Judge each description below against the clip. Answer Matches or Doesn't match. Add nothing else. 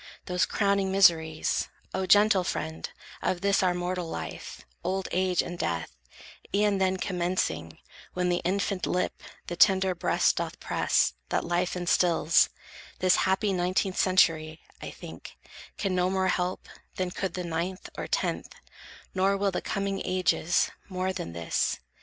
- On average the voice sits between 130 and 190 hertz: Matches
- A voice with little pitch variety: Matches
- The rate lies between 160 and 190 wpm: Doesn't match